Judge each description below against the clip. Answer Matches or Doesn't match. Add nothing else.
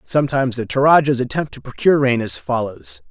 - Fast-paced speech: Doesn't match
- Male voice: Matches